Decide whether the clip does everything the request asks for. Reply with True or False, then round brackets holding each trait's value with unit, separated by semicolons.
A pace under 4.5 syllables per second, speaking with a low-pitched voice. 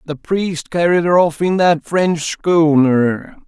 False (3.4 syllables/s; 165 Hz)